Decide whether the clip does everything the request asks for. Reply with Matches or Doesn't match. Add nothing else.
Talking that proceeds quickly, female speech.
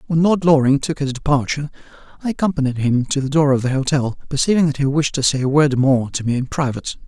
Doesn't match